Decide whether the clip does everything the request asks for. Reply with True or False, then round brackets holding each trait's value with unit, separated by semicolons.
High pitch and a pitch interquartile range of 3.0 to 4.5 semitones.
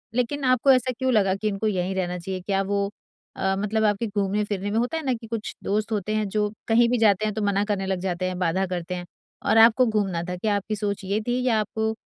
False (205 Hz; 2.6 semitones)